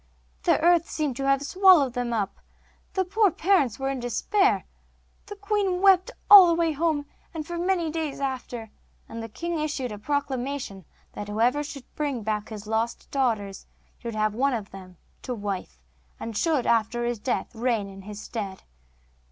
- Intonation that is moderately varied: No, wide, 6.9 semitones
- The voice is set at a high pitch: Yes, very high, 265 Hz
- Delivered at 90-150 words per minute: No, average, 175 wpm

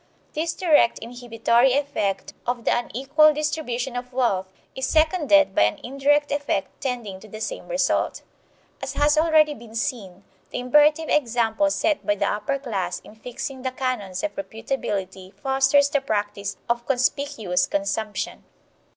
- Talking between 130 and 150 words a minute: Yes, average, 145 wpm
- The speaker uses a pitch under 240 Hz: No, very high, 250 Hz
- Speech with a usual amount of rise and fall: Yes, average, 5.0 semitones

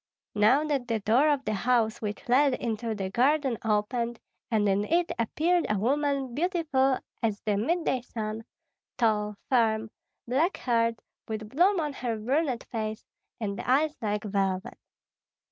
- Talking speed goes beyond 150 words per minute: No, average, 145 wpm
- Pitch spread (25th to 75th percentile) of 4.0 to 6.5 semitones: Yes, average, 4.5 semitones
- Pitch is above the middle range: Yes, high, 235 Hz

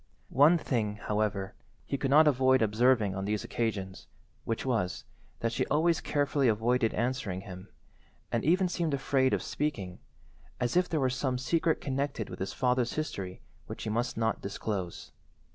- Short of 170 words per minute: Yes, average, 160 wpm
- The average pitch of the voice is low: Yes, low, 125 Hz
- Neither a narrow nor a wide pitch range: Yes, average, 4.9 semitones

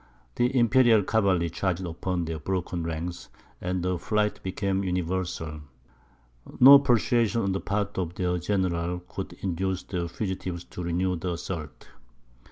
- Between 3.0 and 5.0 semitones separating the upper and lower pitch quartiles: No, narrow, 2.5 semitones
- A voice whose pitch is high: No, very low, 90 Hz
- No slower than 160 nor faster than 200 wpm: No, average, 140 wpm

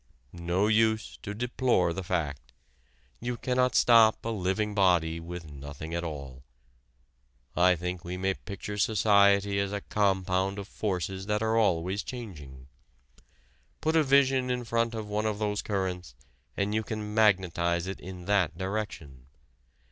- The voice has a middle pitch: No, low, 100 Hz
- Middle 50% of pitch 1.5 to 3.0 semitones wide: No, average, 3.7 semitones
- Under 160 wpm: Yes, average, 150 wpm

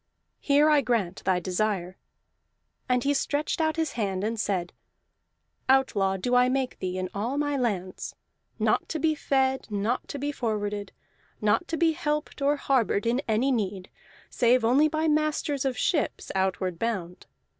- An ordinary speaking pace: Yes, average, 160 wpm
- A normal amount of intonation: No, wide, 6.3 semitones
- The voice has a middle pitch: No, high, 245 Hz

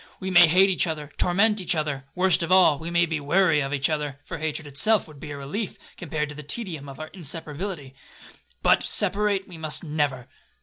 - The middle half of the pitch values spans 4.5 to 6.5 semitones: No, average, 3.9 semitones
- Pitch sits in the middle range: Yes, medium, 160 Hz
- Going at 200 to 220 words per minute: Yes, fast, 205 wpm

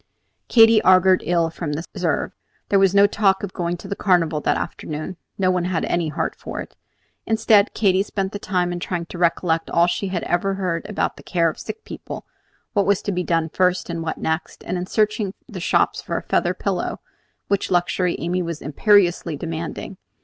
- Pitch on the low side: No, medium, 180 Hz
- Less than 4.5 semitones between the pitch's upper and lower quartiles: Yes, narrow, 2.6 semitones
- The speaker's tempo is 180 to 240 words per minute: Yes, average, 200 wpm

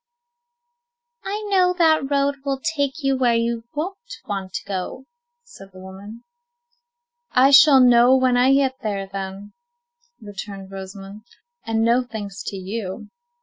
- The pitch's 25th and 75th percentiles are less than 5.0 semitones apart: No, wide, 5.6 semitones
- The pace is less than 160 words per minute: Yes, average, 140 wpm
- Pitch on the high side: Yes, high, 235 Hz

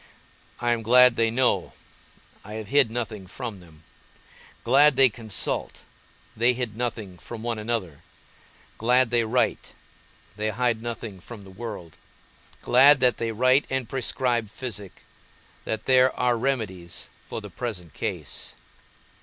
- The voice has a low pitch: Yes, low, 115 Hz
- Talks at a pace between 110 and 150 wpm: Yes, slow, 135 wpm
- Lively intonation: No, average, 2.9 semitones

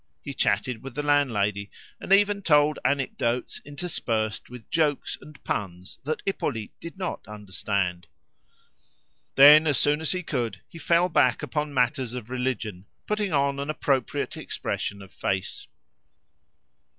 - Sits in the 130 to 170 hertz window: Yes, low, 135 Hz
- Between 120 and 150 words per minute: Yes, average, 140 wpm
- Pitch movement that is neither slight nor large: No, wide, 5.9 semitones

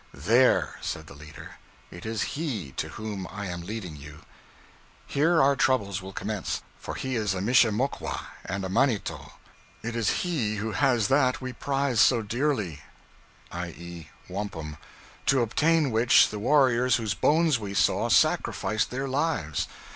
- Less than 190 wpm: Yes, average, 150 wpm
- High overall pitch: No, low, 110 Hz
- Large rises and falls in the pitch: Yes, wide, 5.7 semitones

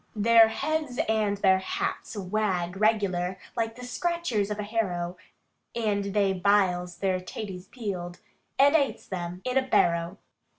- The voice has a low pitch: No, high, 205 Hz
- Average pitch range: Yes, average, 3.7 semitones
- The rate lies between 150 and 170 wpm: No, average, 140 wpm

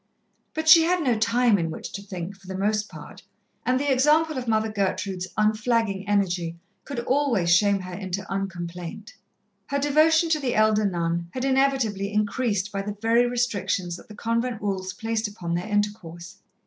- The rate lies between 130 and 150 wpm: No, average, 175 wpm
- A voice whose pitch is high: Yes, high, 210 Hz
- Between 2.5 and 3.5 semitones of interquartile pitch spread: No, average, 4.4 semitones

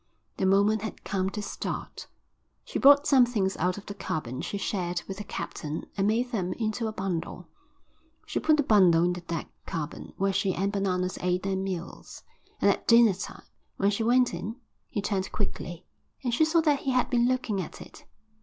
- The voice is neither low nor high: No, high, 200 Hz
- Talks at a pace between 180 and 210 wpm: Yes, average, 200 wpm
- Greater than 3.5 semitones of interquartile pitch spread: Yes, average, 4.3 semitones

